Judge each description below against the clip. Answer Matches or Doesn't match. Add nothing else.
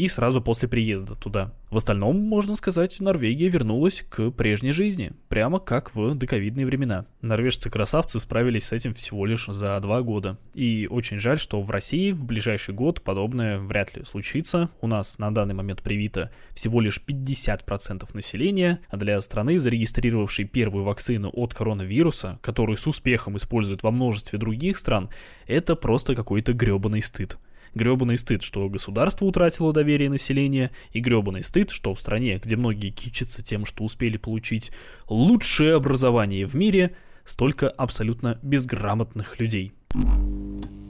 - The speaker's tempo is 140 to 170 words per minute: Matches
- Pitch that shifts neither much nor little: Matches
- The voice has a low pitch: Matches